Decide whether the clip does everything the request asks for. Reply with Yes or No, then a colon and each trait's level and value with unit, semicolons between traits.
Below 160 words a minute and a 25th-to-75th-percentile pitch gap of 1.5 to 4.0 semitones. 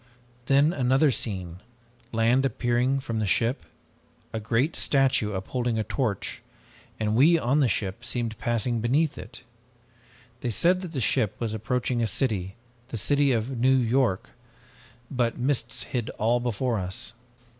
Yes: average, 145 wpm; average, 3.2 semitones